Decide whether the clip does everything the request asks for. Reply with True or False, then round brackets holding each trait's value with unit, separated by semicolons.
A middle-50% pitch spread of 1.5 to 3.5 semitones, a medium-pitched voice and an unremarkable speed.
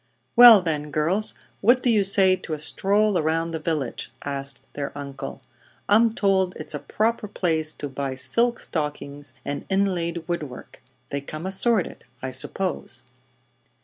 False (5.5 semitones; 170 Hz; 150 wpm)